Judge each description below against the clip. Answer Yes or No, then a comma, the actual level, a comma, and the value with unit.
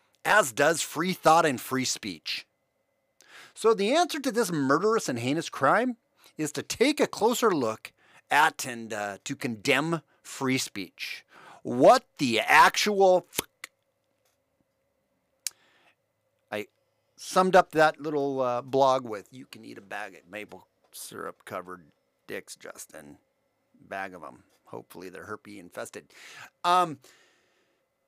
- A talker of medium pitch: Yes, medium, 145 Hz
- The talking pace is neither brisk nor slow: No, slow, 120 wpm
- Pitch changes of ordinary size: No, wide, 6.0 semitones